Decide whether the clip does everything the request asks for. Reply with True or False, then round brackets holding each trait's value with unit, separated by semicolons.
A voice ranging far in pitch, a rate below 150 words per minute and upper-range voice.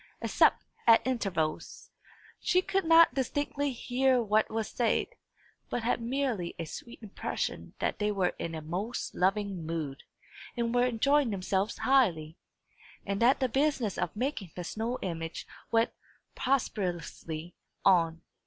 True (6.2 semitones; 135 wpm; 220 Hz)